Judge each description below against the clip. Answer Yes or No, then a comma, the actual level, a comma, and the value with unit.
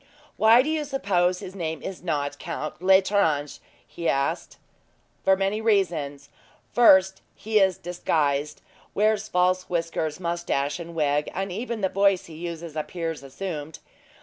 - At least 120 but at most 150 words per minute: Yes, average, 140 wpm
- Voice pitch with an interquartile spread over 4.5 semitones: No, average, 3.9 semitones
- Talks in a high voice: No, medium, 175 Hz